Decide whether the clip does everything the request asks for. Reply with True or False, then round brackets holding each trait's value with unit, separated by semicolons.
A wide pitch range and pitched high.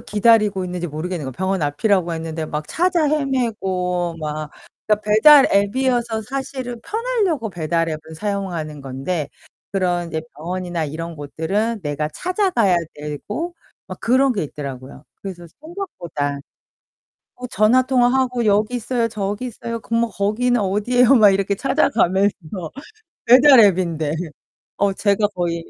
True (6.6 semitones; 200 Hz)